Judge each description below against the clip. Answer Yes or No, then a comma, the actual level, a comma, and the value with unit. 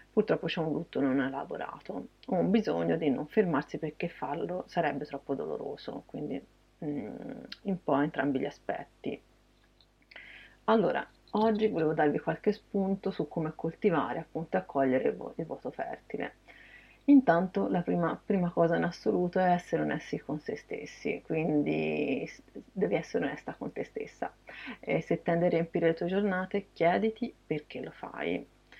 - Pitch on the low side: No, medium, 170 Hz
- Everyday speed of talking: Yes, average, 150 wpm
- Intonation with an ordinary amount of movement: Yes, average, 4.7 semitones